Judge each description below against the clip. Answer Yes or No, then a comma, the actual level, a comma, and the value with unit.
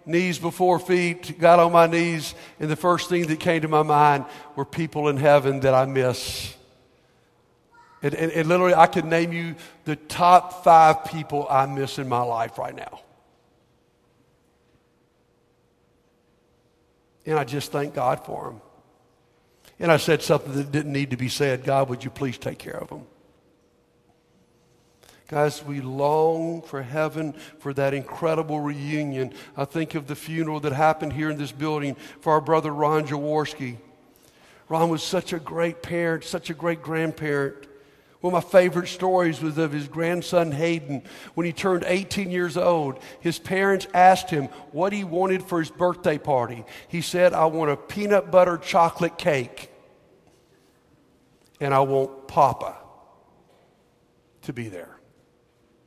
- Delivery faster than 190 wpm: No, average, 155 wpm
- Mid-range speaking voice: Yes, medium, 155 Hz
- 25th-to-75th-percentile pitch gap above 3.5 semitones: No, average, 3.2 semitones